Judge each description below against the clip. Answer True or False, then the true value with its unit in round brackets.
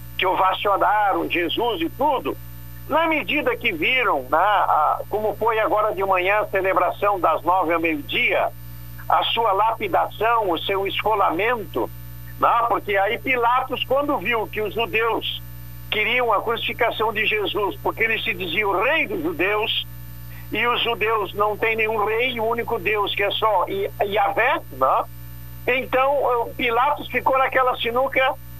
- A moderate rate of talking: True (140 wpm)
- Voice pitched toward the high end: True (215 Hz)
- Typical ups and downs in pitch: False (6.1 semitones)